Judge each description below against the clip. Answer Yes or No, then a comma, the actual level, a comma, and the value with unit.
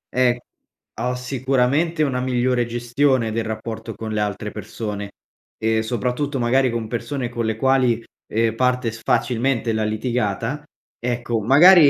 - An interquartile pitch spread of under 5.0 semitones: Yes, narrow, 2.6 semitones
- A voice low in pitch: Yes, low, 120 Hz